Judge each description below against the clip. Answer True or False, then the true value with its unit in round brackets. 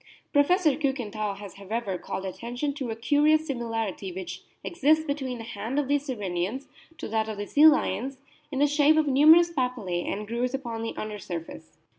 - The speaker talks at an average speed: True (180 wpm)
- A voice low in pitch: False (245 Hz)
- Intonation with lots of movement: True (5.8 semitones)